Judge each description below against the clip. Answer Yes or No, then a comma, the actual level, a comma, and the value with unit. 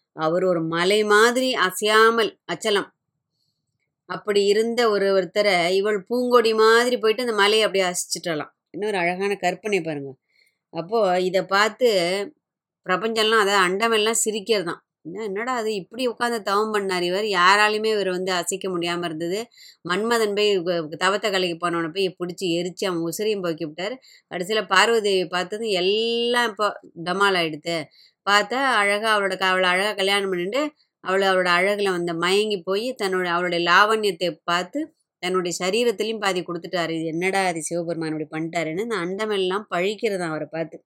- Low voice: No, high, 190 Hz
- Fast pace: Yes, fast, 140 wpm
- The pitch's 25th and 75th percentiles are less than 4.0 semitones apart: Yes, average, 3.5 semitones